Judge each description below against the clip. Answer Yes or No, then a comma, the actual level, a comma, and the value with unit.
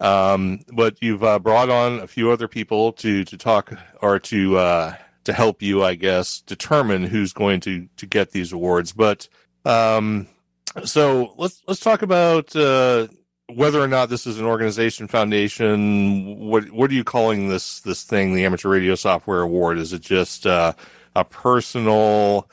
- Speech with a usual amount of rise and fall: Yes, average, 3.5 semitones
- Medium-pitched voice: No, low, 105 Hz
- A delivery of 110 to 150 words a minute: No, average, 170 wpm